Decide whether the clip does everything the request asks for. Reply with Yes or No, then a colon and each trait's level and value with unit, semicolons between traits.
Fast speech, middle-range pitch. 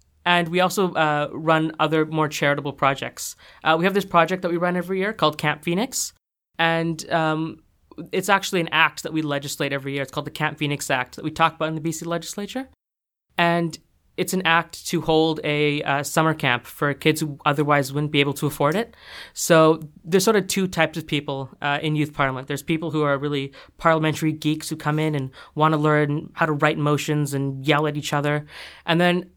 Yes: fast, 210 wpm; medium, 155 Hz